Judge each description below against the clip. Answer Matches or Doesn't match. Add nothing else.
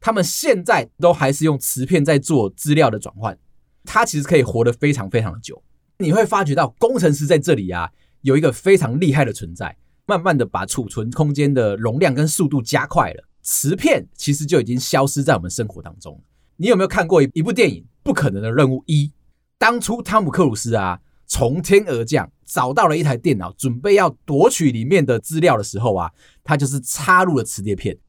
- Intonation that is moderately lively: Doesn't match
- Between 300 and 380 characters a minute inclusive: Matches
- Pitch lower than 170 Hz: Matches